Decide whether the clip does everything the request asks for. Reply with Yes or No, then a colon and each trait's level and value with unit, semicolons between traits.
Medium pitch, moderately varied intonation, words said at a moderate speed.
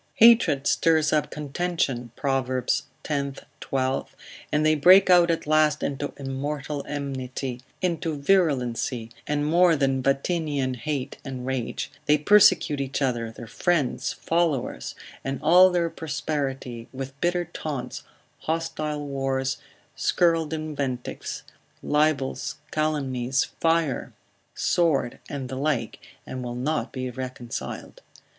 No: medium, 145 Hz; average, 3.2 semitones; slow, 115 wpm